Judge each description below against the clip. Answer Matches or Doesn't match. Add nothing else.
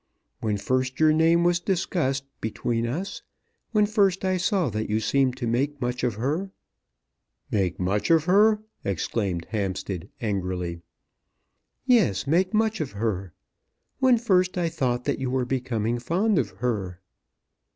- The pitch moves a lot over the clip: Matches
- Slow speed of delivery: Doesn't match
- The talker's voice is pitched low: Matches